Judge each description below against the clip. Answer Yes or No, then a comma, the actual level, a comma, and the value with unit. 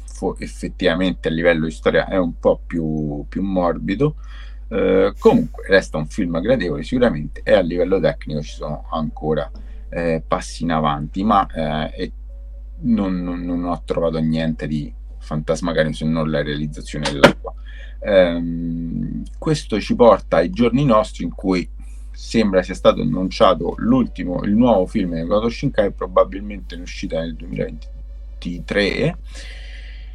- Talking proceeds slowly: No, average, 135 wpm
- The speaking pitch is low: Yes, very low, 80 Hz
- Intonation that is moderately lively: No, wide, 6.7 semitones